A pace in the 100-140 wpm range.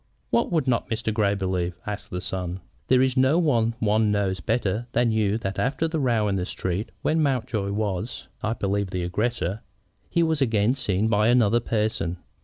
No: average, 190 wpm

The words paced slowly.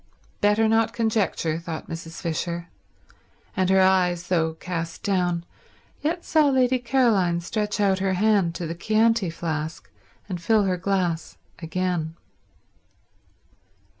Yes: slow, 125 wpm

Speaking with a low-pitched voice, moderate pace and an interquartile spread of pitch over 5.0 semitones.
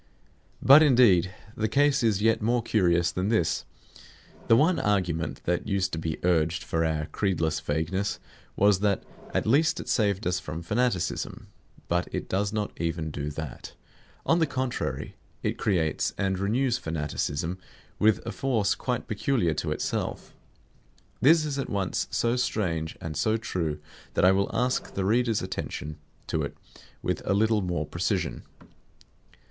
Yes: low, 100 Hz; average, 155 wpm; wide, 5.4 semitones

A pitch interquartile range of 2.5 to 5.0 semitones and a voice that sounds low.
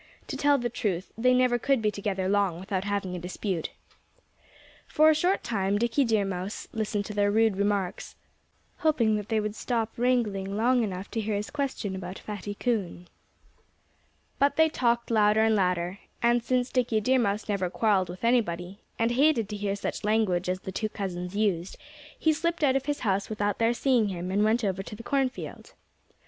No: average, 3.7 semitones; high, 210 Hz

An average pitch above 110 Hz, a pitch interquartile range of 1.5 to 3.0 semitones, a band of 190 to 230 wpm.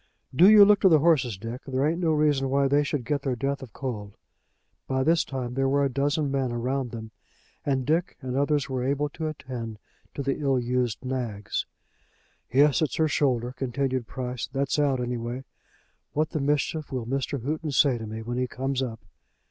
Yes: low, 135 Hz; average, 2.7 semitones; average, 200 wpm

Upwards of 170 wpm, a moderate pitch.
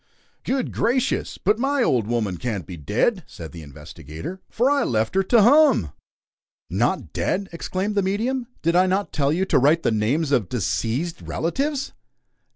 No: average, 165 wpm; medium, 170 Hz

